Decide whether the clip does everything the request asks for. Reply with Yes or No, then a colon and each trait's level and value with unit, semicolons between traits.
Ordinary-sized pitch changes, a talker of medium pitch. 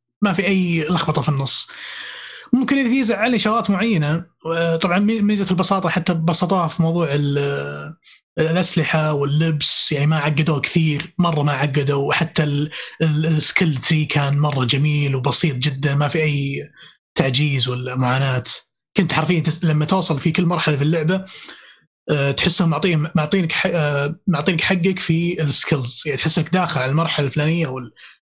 Yes: average, 3.6 semitones; medium, 160 Hz